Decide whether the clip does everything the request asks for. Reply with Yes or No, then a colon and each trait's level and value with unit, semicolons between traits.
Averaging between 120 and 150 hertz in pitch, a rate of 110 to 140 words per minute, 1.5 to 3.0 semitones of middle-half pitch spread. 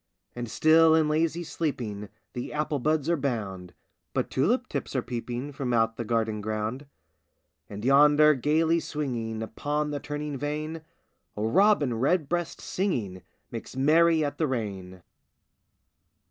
No: medium, 140 Hz; slow, 135 wpm; wide, 5.5 semitones